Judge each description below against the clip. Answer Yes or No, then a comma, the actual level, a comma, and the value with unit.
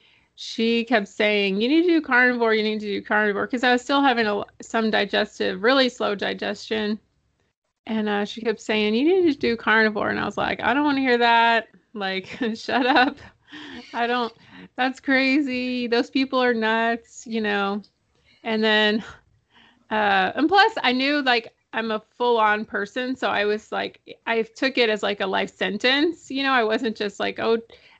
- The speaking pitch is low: No, high, 230 Hz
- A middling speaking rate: Yes, average, 190 wpm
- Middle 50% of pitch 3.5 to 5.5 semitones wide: No, average, 2.9 semitones